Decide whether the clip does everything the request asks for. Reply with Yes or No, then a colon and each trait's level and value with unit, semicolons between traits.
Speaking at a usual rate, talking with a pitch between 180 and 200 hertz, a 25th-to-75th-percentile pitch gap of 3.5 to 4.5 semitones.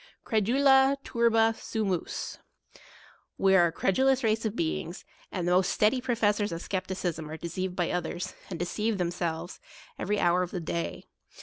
Yes: average, 160 wpm; high, 190 Hz; average, 4.2 semitones